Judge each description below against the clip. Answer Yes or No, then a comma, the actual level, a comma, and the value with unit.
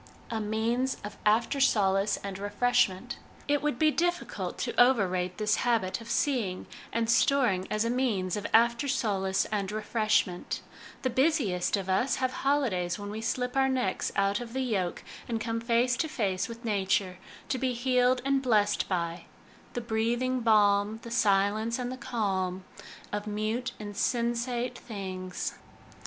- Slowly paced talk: No, average, 155 wpm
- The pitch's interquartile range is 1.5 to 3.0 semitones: No, average, 3.8 semitones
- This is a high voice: Yes, high, 225 Hz